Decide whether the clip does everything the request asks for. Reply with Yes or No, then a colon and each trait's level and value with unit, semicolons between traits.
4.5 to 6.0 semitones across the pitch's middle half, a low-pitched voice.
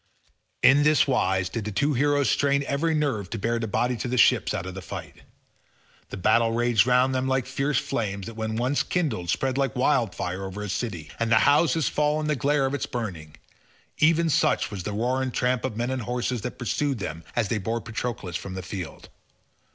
Yes: average, 5.1 semitones; low, 120 Hz